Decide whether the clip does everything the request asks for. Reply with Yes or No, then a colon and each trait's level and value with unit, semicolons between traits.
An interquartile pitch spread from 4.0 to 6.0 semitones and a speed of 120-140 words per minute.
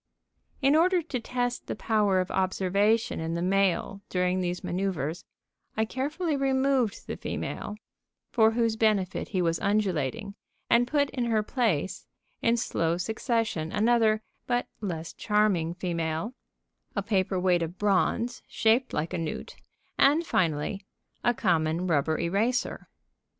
Yes: average, 5.0 semitones; slow, 135 wpm